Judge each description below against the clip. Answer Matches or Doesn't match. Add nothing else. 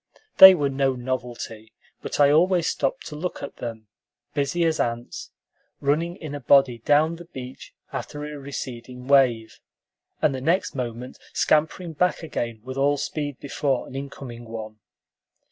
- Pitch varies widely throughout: Doesn't match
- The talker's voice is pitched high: Doesn't match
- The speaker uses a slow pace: Doesn't match